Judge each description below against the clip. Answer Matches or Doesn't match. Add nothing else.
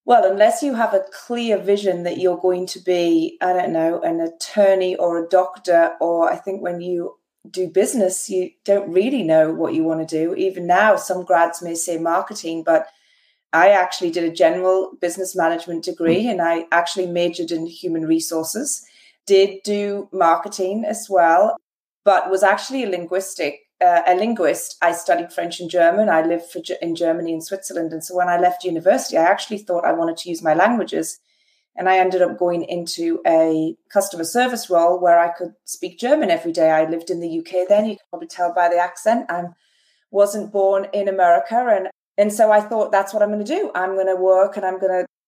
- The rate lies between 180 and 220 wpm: Matches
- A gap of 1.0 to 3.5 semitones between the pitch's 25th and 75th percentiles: Matches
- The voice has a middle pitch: Matches